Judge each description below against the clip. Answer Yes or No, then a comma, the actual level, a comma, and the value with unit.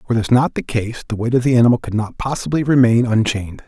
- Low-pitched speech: Yes, low, 120 Hz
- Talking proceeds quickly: Yes, fast, 245 wpm